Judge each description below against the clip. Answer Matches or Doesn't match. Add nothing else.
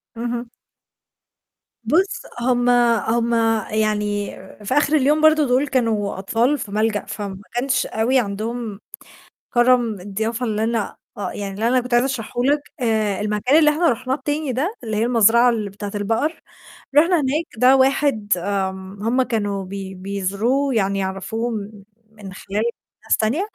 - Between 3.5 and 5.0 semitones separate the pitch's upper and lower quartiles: Matches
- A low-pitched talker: Doesn't match